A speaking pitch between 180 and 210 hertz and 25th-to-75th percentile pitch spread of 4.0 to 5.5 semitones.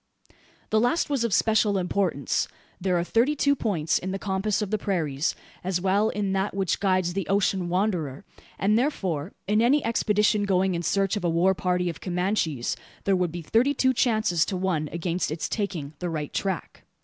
No: high, 190 Hz; average, 3.4 semitones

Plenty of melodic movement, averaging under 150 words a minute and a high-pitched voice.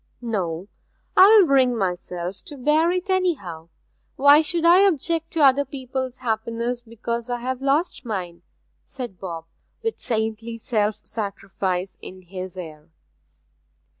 Yes: wide, 7.0 semitones; slow, 135 wpm; high, 235 Hz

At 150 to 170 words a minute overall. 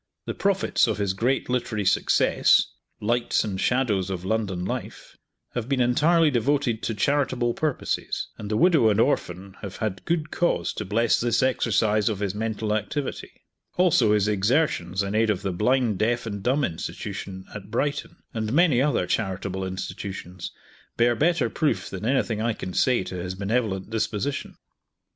Yes: average, 160 wpm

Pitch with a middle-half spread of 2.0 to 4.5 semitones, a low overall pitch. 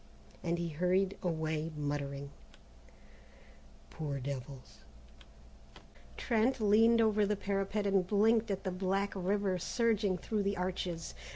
No: average, 4.0 semitones; high, 190 Hz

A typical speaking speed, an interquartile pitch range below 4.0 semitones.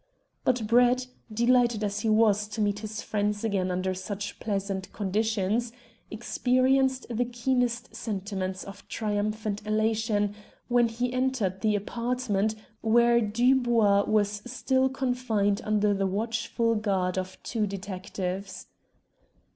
No: slow, 120 wpm; average, 2.9 semitones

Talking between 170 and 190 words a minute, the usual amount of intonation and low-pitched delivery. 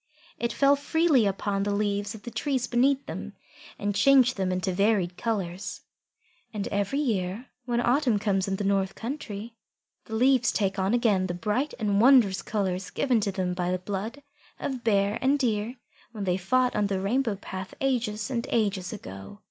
No: average, 180 wpm; average, 4.1 semitones; high, 210 Hz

